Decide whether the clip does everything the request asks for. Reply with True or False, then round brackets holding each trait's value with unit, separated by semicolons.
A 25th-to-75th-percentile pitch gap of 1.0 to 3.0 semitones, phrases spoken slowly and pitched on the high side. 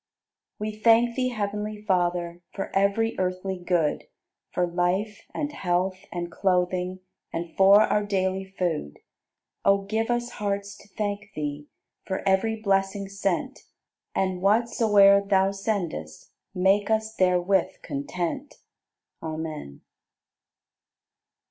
True (2.6 semitones; 115 wpm; 195 Hz)